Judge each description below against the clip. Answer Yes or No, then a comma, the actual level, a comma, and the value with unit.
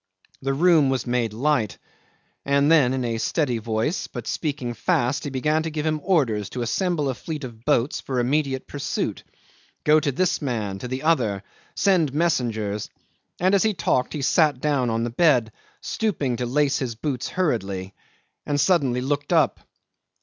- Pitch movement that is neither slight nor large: Yes, average, 4.3 semitones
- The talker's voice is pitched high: No, low, 135 Hz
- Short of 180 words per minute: Yes, average, 170 wpm